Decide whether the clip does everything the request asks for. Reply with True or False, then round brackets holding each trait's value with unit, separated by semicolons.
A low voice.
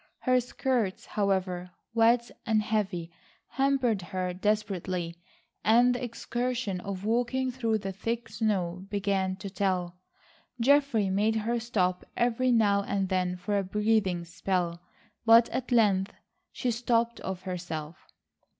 False (205 Hz)